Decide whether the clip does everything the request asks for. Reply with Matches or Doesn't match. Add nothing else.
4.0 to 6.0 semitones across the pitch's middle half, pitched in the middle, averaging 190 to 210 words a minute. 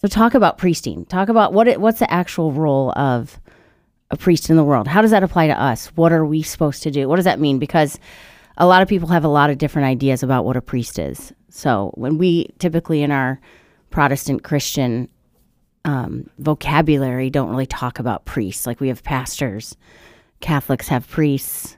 Matches